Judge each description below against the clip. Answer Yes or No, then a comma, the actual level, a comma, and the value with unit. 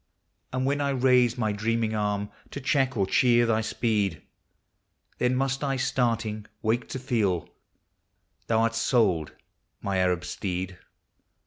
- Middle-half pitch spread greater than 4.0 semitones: No, average, 3.7 semitones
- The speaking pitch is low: Yes, low, 115 Hz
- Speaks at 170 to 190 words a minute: No, average, 140 wpm